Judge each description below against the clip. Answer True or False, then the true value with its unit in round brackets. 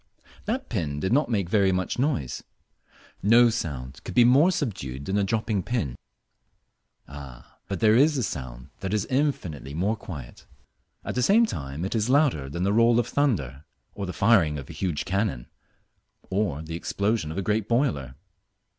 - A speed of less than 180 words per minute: True (170 wpm)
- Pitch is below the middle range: True (100 Hz)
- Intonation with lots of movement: True (8.1 semitones)